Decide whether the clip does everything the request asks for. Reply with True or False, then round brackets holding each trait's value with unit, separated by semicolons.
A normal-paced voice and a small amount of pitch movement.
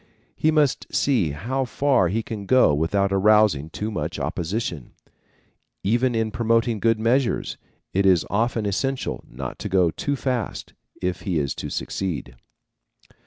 False (145 wpm; 4.9 semitones)